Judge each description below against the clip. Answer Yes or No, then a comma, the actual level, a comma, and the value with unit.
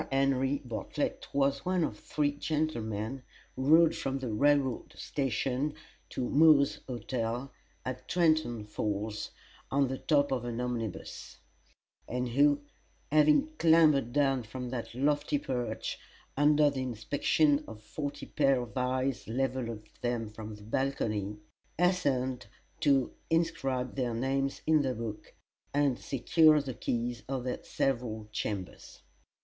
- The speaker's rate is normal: No, slow, 130 wpm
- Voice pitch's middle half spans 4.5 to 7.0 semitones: No, average, 3.5 semitones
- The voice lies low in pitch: Yes, low, 130 Hz